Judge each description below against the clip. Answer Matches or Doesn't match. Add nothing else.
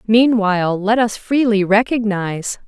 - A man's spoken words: Doesn't match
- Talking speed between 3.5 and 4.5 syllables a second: Matches